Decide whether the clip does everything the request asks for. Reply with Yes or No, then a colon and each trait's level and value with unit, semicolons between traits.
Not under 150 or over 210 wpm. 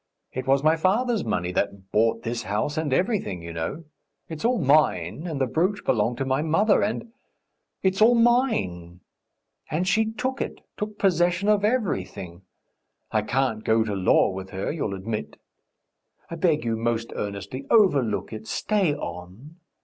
Yes: average, 160 wpm